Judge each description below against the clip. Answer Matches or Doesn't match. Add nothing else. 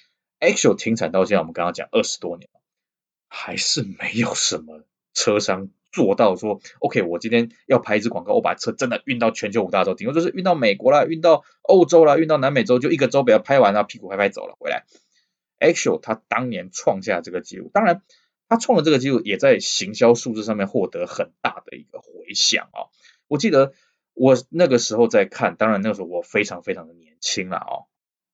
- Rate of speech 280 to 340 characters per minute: Matches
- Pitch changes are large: Matches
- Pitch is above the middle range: Doesn't match